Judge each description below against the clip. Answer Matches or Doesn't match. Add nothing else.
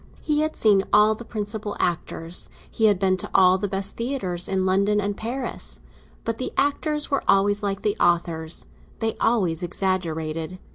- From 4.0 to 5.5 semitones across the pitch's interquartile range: Doesn't match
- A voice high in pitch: Matches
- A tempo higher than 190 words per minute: Doesn't match